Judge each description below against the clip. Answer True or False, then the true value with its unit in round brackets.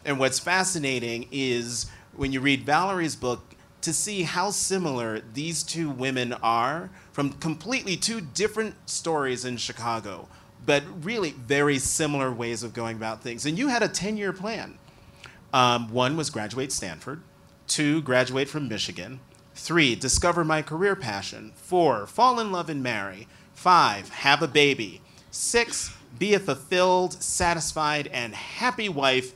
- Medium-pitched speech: True (145 Hz)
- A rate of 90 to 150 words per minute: True (145 wpm)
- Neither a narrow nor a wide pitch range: False (6.0 semitones)